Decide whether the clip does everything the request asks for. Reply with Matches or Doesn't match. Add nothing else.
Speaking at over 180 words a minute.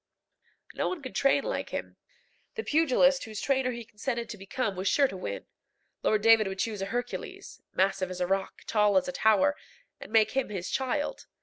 Matches